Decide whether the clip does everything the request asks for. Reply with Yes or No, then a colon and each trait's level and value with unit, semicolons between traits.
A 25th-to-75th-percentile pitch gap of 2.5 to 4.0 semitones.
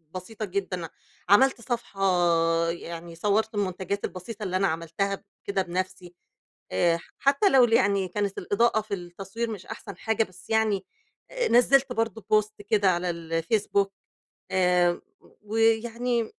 Yes: average, 3.5 semitones